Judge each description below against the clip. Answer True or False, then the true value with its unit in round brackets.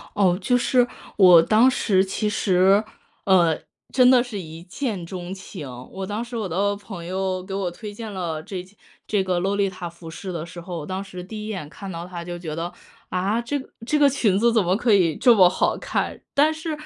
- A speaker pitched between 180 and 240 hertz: True (190 Hz)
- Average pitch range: True (3.6 semitones)